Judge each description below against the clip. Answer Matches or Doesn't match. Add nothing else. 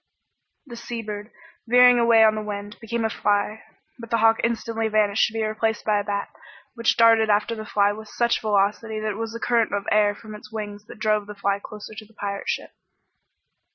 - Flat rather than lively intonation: Matches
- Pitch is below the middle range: Doesn't match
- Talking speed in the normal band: Doesn't match